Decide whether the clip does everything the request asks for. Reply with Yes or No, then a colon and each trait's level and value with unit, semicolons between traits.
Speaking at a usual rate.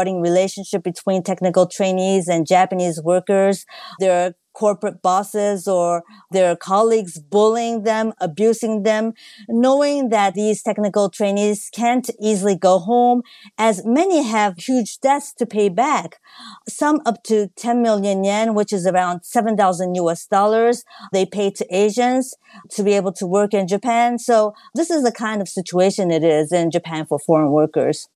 Yes: average, 150 wpm